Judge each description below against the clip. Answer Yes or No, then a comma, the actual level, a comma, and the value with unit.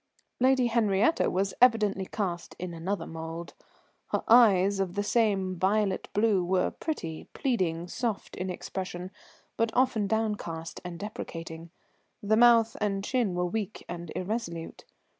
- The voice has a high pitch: Yes, high, 195 Hz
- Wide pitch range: No, average, 4.0 semitones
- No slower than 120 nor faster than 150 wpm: Yes, slow, 135 wpm